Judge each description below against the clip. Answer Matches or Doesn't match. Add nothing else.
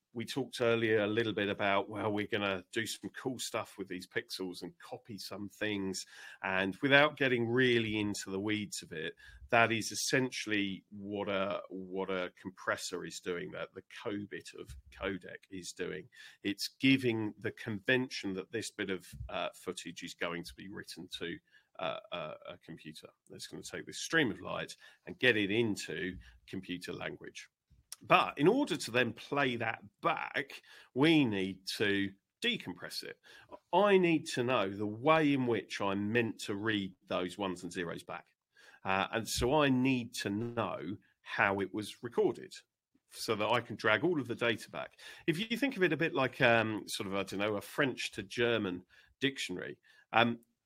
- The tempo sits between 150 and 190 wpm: Matches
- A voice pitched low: Matches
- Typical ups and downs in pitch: Matches